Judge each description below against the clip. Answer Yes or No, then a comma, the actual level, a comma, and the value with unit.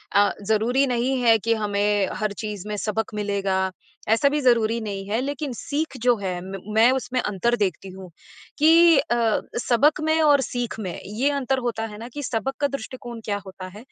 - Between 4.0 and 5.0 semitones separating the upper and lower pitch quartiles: Yes, average, 4.3 semitones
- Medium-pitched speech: No, high, 230 Hz